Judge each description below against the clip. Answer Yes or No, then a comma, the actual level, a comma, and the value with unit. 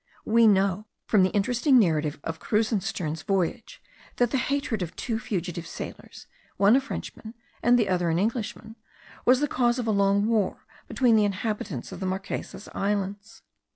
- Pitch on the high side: Yes, high, 210 Hz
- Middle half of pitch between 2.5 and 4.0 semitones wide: Yes, average, 3.6 semitones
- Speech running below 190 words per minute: Yes, average, 165 wpm